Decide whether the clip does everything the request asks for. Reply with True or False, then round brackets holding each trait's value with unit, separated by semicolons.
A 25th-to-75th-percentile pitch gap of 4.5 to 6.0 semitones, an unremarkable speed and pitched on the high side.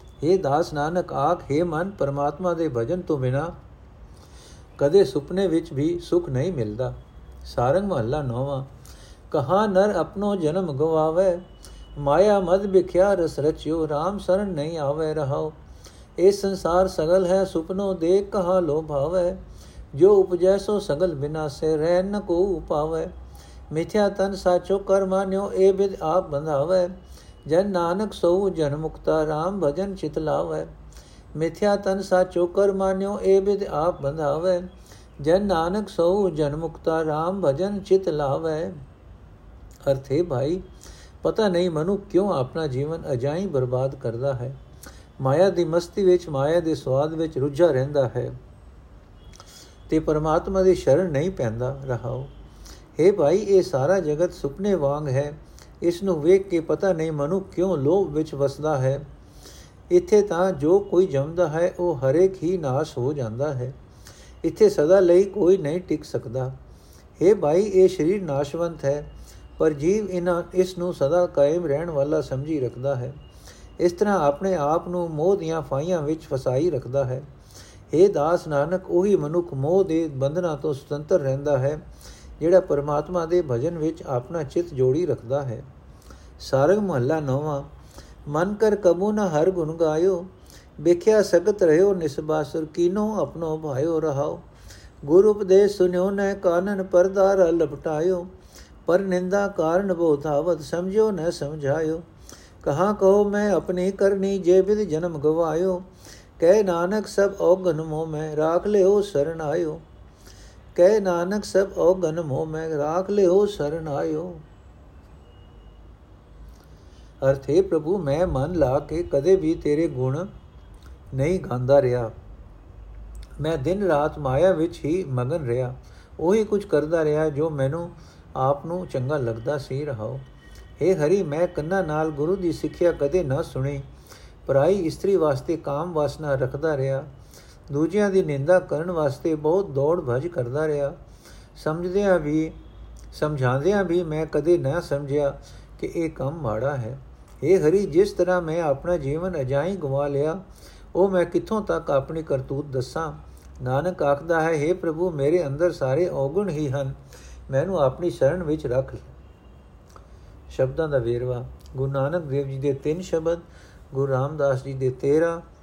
False (5.1 semitones; 145 wpm; 160 Hz)